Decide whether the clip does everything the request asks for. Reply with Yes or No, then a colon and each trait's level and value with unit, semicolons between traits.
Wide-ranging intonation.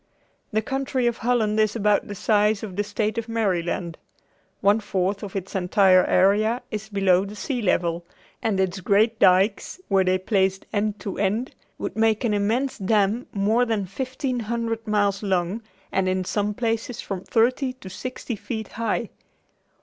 No: average, 2.8 semitones